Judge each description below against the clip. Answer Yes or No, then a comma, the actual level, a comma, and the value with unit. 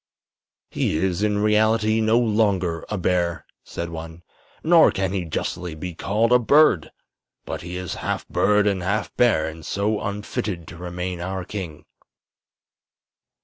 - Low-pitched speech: Yes, very low, 95 Hz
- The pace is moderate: Yes, average, 145 wpm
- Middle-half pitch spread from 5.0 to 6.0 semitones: No, average, 3.6 semitones